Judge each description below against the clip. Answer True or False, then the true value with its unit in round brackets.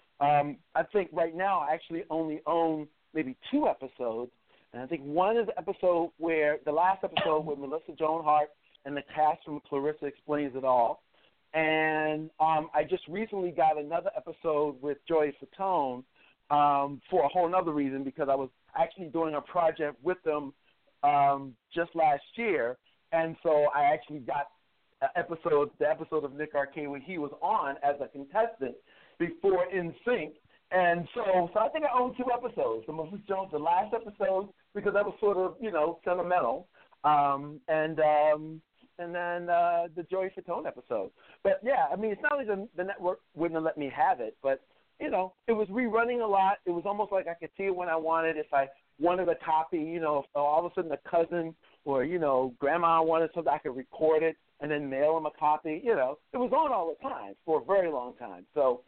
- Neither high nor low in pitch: True (160 Hz)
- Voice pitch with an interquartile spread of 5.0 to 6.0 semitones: False (3.9 semitones)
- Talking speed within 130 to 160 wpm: False (200 wpm)